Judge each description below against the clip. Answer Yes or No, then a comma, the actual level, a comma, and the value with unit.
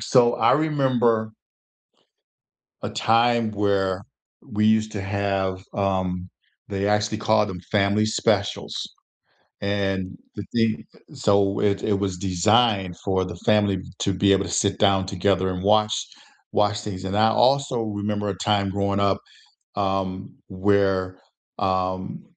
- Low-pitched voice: Yes, low, 100 Hz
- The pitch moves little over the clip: Yes, narrow, 1.9 semitones